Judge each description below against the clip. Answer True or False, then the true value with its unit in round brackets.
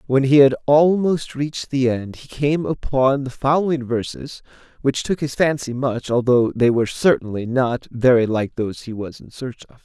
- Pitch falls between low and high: False (130 Hz)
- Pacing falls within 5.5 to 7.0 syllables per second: False (4.9 syllables/s)